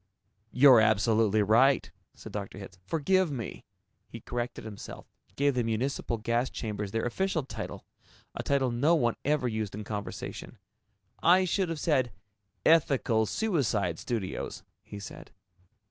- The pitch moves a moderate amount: Yes, average, 4.8 semitones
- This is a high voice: No, low, 120 Hz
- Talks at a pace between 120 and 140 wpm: Yes, slow, 135 wpm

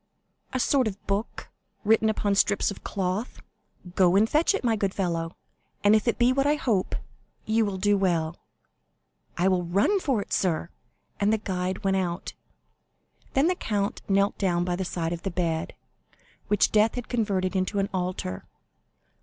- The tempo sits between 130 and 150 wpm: No, average, 175 wpm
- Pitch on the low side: No, high, 200 Hz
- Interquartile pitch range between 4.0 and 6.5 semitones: No, average, 3.2 semitones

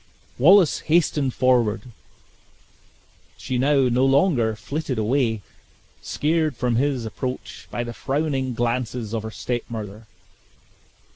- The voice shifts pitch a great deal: No, average, 3.5 semitones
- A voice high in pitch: No, low, 125 Hz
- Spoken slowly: Yes, slow, 115 wpm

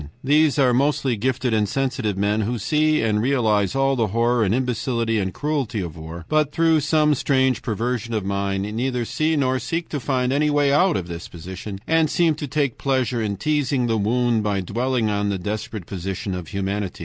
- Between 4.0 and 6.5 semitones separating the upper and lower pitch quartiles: Yes, average, 5.2 semitones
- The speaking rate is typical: Yes, average, 195 wpm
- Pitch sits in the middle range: No, low, 120 Hz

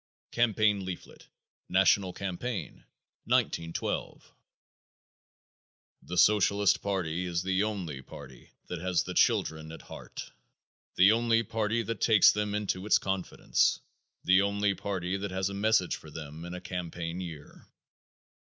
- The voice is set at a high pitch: No, very low, 95 Hz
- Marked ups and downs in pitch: No, average, 2.8 semitones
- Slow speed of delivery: Yes, slow, 130 wpm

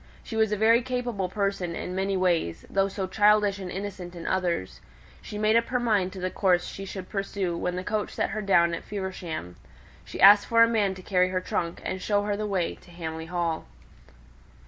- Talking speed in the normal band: No, fast, 215 wpm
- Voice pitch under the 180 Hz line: No, high, 195 Hz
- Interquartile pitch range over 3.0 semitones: No, average, 2.7 semitones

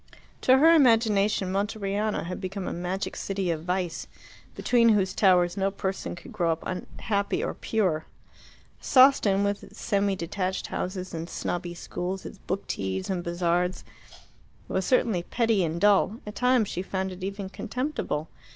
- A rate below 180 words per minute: Yes, average, 155 wpm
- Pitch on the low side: No, high, 195 Hz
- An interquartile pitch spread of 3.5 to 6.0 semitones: No, average, 3.0 semitones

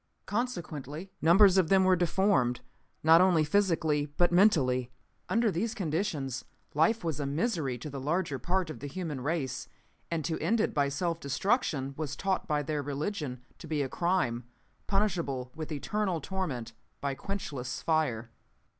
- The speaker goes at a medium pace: Yes, average, 155 wpm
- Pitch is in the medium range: Yes, medium, 160 Hz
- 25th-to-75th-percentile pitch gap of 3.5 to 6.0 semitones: Yes, average, 5.2 semitones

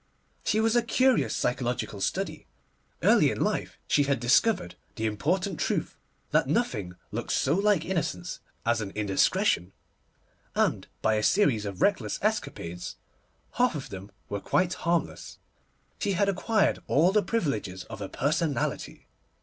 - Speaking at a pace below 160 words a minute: Yes, average, 140 wpm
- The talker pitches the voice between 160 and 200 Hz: No, medium, 145 Hz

